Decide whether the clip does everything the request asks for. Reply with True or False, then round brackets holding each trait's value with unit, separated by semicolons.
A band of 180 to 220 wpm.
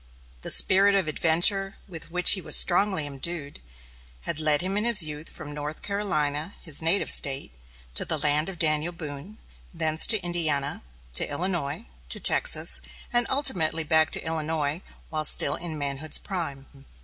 False (160 wpm)